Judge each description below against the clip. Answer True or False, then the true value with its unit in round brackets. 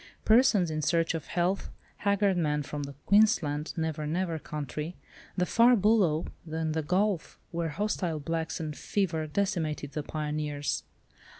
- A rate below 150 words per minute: True (140 wpm)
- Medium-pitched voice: True (165 Hz)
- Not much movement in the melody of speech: False (4.0 semitones)